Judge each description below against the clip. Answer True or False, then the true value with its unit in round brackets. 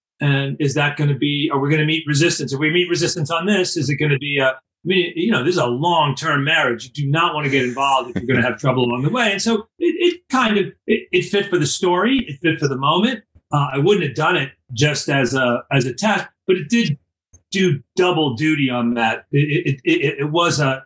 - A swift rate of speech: True (270 wpm)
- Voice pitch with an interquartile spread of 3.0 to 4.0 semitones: False (4.7 semitones)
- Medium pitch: True (150 Hz)